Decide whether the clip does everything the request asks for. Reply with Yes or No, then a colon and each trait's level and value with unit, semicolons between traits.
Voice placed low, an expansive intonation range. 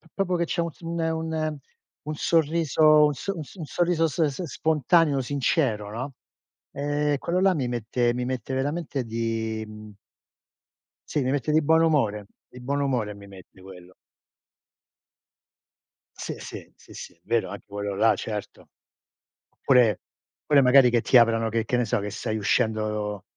Yes: low, 130 Hz; wide, 5.8 semitones